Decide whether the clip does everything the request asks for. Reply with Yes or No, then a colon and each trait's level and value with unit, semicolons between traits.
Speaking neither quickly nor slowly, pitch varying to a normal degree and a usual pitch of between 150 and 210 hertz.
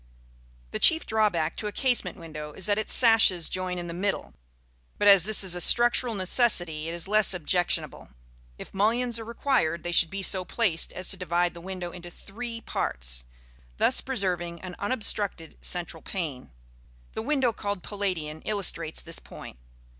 Yes: average, 170 wpm; average, 4.1 semitones; medium, 185 Hz